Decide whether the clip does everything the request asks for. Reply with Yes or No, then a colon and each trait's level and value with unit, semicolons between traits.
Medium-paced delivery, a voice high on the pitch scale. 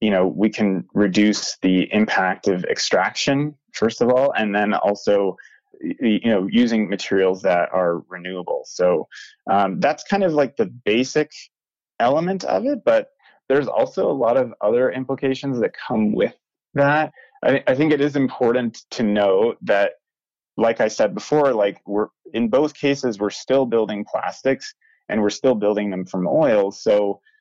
No: average, 165 wpm; low, 115 Hz